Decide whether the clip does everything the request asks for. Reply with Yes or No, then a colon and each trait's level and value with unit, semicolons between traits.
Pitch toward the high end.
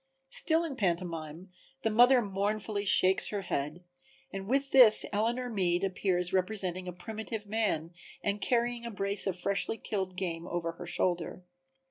Yes: high, 195 Hz